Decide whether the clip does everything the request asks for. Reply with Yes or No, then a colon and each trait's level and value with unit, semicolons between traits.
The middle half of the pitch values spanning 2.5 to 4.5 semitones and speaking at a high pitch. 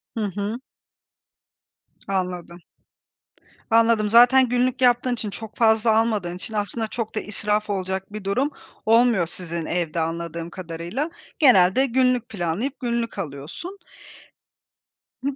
No: average, 4.9 semitones; high, 215 Hz